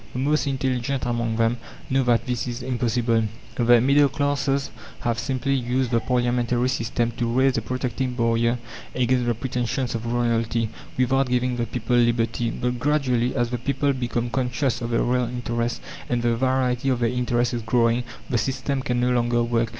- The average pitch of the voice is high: No, low, 120 Hz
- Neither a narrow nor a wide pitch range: No, narrow, 1.5 semitones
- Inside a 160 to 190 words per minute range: Yes, average, 180 wpm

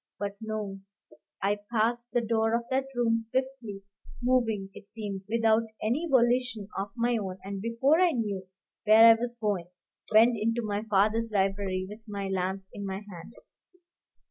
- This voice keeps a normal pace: Yes, average, 160 wpm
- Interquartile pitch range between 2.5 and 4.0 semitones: Yes, average, 2.9 semitones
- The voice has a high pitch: Yes, high, 220 Hz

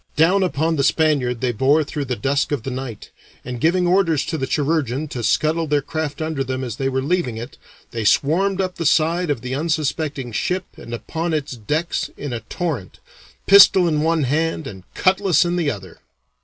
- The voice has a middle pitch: Yes, medium, 150 Hz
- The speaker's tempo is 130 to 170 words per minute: No, average, 195 wpm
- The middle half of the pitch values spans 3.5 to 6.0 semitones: Yes, average, 4.1 semitones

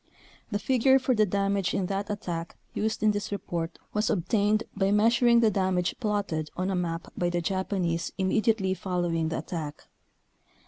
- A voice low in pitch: No, high, 195 Hz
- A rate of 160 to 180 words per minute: Yes, average, 170 wpm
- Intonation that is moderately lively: Yes, average, 3.3 semitones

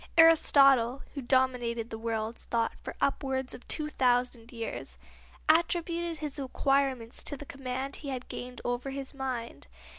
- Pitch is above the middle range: Yes, very high, 260 Hz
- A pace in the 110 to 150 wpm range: Yes, average, 145 wpm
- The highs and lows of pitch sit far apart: No, narrow, 2.6 semitones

